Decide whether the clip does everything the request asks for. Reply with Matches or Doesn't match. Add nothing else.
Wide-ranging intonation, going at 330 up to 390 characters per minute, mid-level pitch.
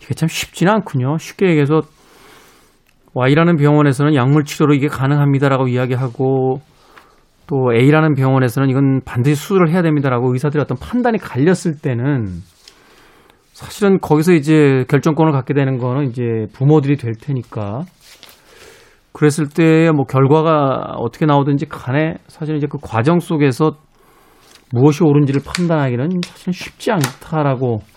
Doesn't match